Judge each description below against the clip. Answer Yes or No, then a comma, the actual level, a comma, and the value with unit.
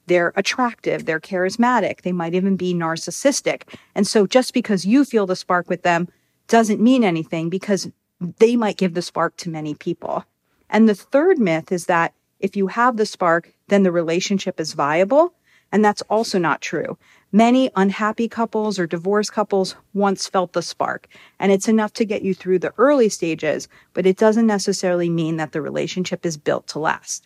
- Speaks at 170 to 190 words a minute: Yes, average, 185 wpm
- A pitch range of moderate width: Yes, average, 3.6 semitones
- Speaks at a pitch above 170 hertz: Yes, high, 190 Hz